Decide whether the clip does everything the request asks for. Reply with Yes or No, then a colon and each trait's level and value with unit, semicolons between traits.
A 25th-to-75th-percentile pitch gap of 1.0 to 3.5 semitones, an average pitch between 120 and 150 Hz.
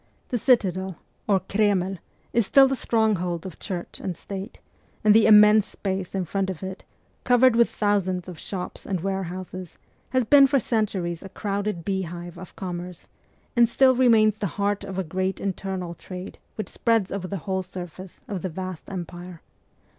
No: average, 2.7 semitones; high, 190 Hz